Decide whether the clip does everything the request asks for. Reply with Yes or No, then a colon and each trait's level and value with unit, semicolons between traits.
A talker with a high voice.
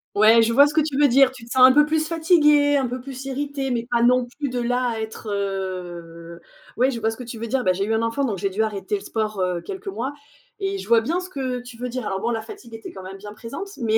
Yes: high, 240 Hz